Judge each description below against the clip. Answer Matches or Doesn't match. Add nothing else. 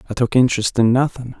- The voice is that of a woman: Doesn't match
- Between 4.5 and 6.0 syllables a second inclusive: Doesn't match